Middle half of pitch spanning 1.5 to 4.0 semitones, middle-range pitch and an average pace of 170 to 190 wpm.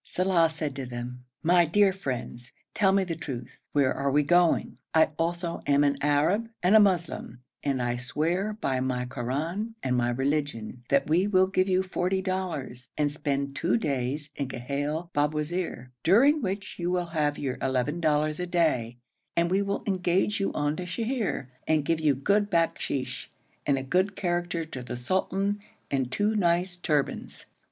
No: average, 5.2 semitones; medium, 160 Hz; average, 175 wpm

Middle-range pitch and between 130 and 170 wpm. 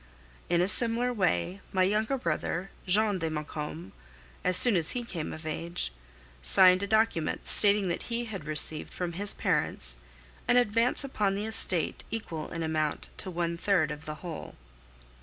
Yes: medium, 180 Hz; average, 160 wpm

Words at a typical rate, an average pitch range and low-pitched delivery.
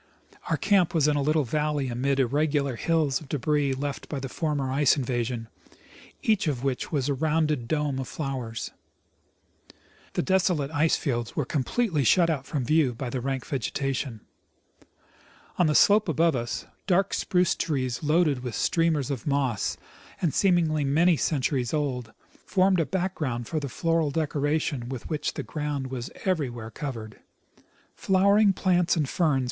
No: average, 160 wpm; average, 3.8 semitones; medium, 145 Hz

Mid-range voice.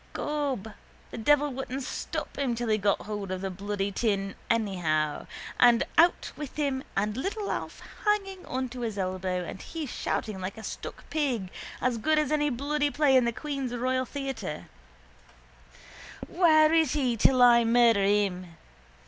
No: high, 245 Hz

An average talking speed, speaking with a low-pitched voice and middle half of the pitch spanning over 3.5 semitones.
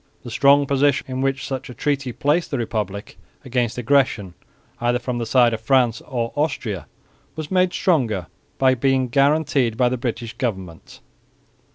No: average, 160 wpm; low, 125 Hz; average, 3.1 semitones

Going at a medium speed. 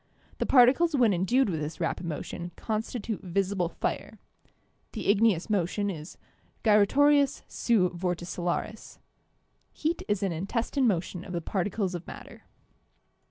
No: slow, 125 wpm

